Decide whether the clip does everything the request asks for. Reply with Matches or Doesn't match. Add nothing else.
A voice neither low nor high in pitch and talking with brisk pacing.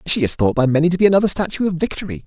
Matches